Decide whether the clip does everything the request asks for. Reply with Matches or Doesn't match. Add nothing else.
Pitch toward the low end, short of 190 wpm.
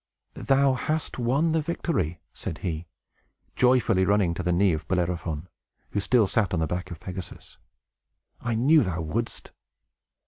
Matches